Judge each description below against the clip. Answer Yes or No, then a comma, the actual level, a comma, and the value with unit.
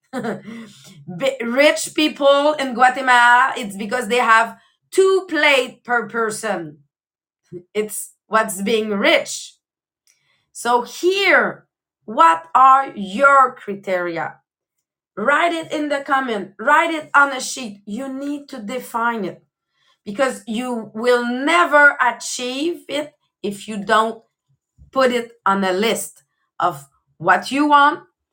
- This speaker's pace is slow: Yes, slow, 115 wpm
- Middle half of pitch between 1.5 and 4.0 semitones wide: No, average, 4.8 semitones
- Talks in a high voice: Yes, high, 245 Hz